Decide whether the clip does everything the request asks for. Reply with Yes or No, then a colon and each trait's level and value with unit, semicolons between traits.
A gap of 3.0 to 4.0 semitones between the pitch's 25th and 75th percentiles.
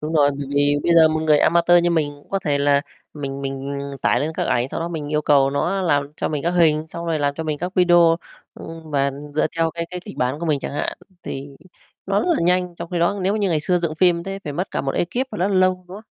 Yes: average, 3.4 semitones